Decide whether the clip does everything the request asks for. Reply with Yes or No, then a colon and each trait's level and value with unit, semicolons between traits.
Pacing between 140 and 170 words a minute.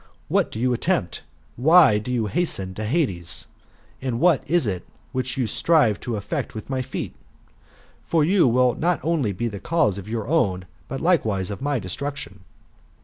No: average, 180 wpm